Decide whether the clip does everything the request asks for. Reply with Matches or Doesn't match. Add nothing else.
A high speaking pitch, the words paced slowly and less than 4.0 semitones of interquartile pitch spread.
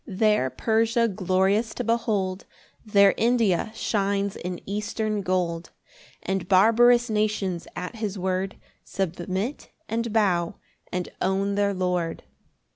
Matches